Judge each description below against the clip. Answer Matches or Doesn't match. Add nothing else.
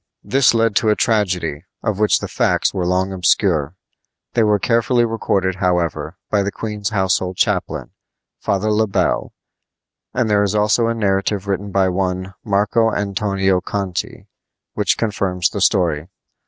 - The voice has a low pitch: Matches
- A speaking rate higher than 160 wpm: Doesn't match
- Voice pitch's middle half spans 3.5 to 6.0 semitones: Doesn't match